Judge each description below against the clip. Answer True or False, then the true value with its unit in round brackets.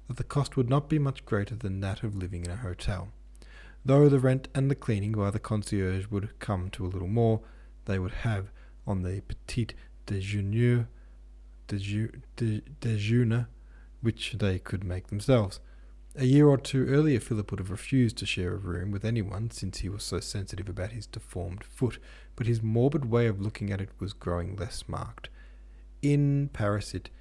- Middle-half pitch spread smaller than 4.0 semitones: False (4.4 semitones)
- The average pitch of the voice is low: True (105 Hz)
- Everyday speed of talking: True (180 wpm)